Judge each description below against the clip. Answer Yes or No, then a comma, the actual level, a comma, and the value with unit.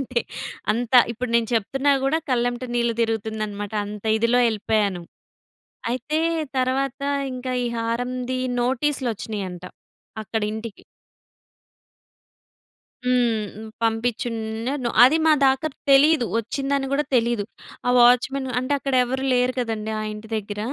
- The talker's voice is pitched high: Yes, high, 240 Hz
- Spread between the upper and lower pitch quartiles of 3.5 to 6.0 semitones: No, average, 2.9 semitones